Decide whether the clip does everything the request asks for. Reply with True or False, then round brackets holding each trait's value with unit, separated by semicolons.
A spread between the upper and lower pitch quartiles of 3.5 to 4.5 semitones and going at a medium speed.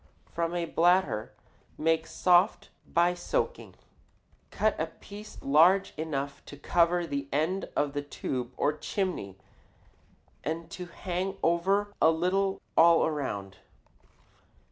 False (3.8 semitones; 120 wpm)